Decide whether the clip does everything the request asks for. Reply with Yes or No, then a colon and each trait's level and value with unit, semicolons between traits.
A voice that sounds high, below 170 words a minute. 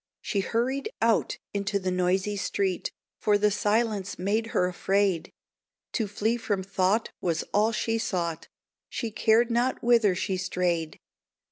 Yes: high, 200 Hz; average, 140 wpm